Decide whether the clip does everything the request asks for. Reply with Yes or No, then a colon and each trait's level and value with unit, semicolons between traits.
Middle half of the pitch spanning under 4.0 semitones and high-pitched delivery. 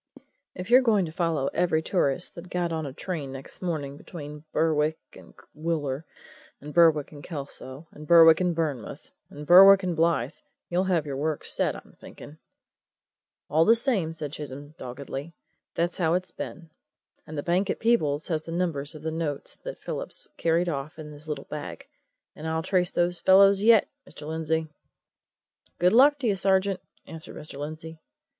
No: average, 3.1 semitones; medium, 160 Hz